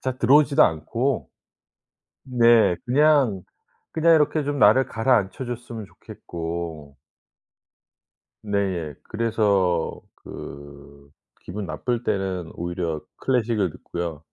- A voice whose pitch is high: No, low, 105 Hz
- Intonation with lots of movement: Yes, wide, 6.5 semitones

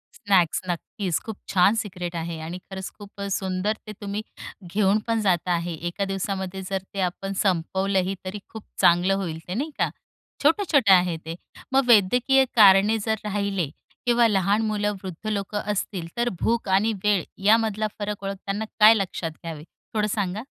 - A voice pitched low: No, high, 195 Hz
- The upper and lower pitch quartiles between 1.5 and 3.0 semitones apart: Yes, narrow, 2.6 semitones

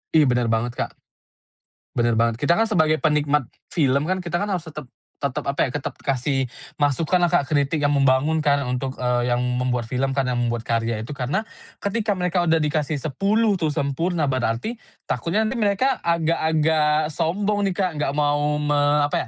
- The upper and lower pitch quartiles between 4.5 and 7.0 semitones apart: Yes, average, 4.8 semitones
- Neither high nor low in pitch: Yes, medium, 150 Hz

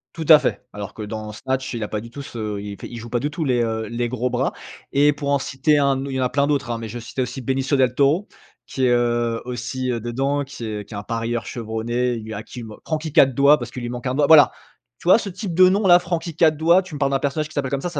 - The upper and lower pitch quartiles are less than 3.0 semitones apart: No, average, 3.8 semitones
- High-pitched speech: No, low, 130 Hz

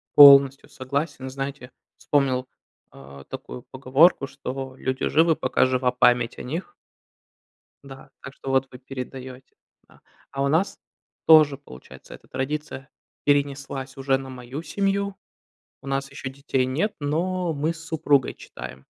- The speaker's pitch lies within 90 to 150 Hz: Yes, low, 135 Hz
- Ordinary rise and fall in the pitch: No, narrow, 2.2 semitones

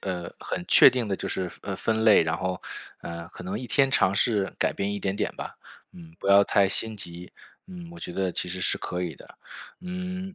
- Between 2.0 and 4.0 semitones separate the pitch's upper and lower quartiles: No, average, 4.7 semitones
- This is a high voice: No, low, 100 Hz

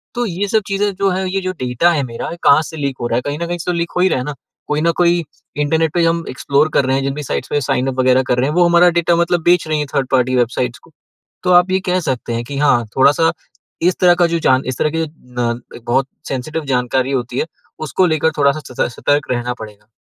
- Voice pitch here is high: No, medium, 150 Hz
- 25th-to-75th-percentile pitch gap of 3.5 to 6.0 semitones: Yes, average, 5.0 semitones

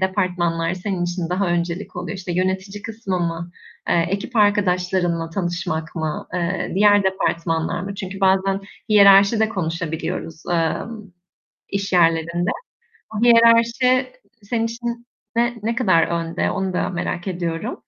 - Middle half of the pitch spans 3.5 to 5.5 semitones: No, average, 3.1 semitones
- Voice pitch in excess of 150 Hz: Yes, medium, 185 Hz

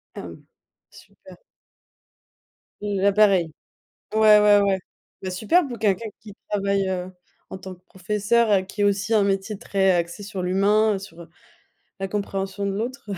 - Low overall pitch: No, high, 200 Hz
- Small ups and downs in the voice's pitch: Yes, narrow, 1.7 semitones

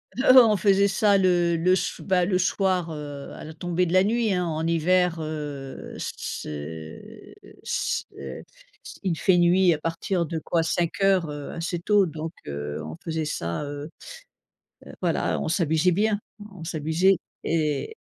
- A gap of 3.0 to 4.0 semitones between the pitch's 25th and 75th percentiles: Yes, average, 3.4 semitones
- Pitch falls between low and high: Yes, medium, 170 Hz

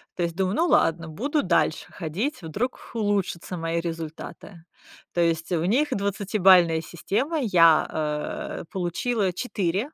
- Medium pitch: Yes, medium, 180 Hz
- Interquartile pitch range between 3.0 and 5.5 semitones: Yes, average, 4.2 semitones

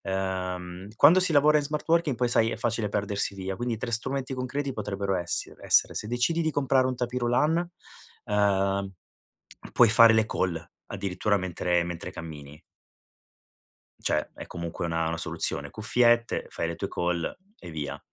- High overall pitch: No, low, 105 Hz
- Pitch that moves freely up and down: Yes, wide, 5.9 semitones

